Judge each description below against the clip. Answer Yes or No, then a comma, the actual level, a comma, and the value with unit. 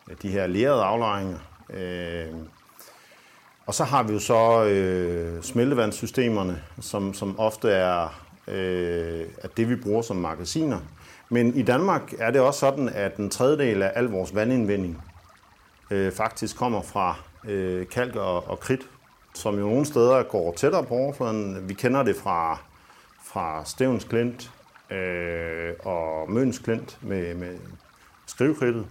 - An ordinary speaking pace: No, slow, 120 wpm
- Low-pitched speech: Yes, low, 100 Hz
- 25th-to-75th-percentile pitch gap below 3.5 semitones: No, average, 4.6 semitones